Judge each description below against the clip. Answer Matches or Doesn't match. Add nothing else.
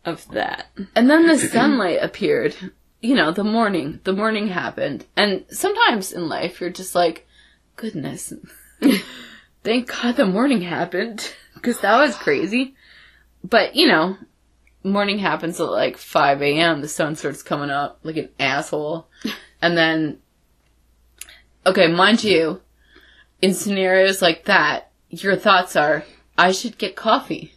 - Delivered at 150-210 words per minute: Doesn't match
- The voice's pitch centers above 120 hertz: Matches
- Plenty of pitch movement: Matches